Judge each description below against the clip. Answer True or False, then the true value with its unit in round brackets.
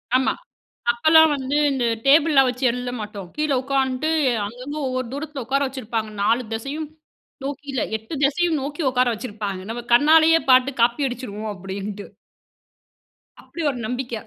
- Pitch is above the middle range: True (255 Hz)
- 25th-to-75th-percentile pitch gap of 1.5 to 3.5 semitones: False (4.0 semitones)